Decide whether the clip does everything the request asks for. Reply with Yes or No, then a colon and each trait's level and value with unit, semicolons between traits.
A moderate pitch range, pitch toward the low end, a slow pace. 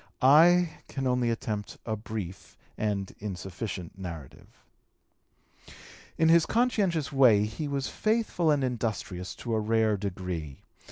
No: wide, 7.1 semitones; low, 110 Hz; slow, 120 wpm